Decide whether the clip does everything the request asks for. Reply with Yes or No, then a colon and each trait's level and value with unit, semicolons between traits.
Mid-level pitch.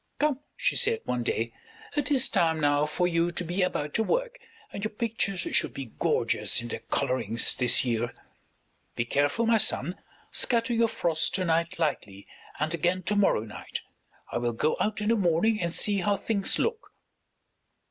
Yes: medium, 175 Hz